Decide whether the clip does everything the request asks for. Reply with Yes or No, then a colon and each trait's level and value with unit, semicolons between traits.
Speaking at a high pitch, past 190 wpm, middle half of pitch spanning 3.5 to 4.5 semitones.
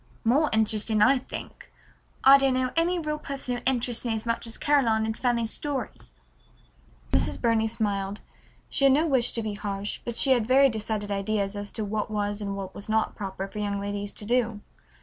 Yes: high, 220 Hz; average, 200 wpm; average, 3.8 semitones